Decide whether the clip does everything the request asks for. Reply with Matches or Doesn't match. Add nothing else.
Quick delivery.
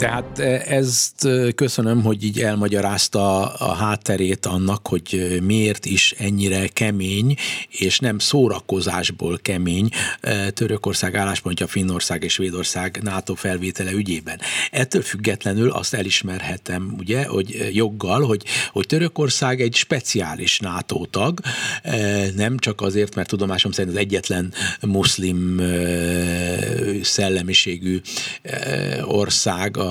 Doesn't match